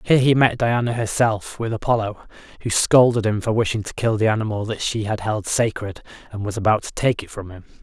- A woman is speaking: No, male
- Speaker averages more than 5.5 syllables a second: Yes, 5.8 syllables/s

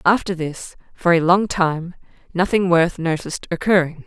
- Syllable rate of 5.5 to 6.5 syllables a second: No, 4.9 syllables/s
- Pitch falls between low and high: Yes, medium, 175 Hz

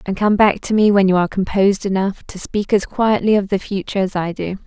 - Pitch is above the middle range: Yes, high, 195 Hz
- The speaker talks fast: Yes, fast, 255 wpm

